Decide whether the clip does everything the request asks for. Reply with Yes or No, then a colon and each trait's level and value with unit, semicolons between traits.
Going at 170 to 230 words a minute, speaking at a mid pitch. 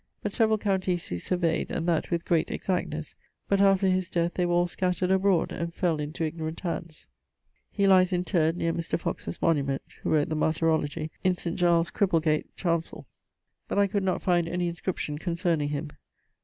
Yes: average, 180 wpm; medium, 170 Hz